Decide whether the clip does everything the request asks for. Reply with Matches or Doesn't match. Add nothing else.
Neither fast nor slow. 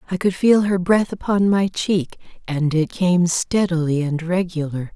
Matches